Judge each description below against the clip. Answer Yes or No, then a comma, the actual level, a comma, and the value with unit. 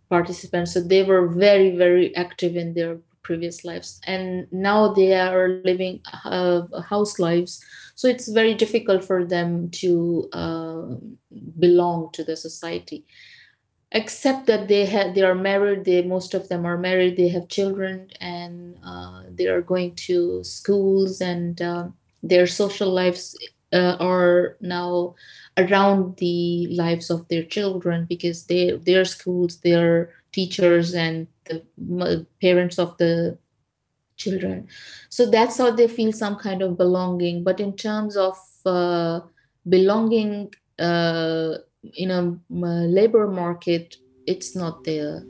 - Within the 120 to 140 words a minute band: Yes, average, 135 wpm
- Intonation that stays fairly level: Yes, narrow, 2.0 semitones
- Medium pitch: Yes, medium, 180 Hz